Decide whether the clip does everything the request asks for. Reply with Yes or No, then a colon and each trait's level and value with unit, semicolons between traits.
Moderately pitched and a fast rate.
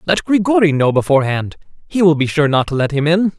Yes: medium, 160 Hz; fast, 230 wpm